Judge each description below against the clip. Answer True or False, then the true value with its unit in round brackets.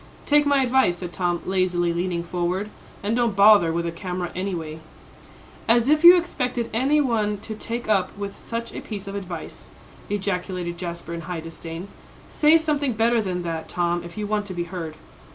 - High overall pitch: True (195 Hz)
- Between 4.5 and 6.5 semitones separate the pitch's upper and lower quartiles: True (4.9 semitones)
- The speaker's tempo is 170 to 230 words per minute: True (185 wpm)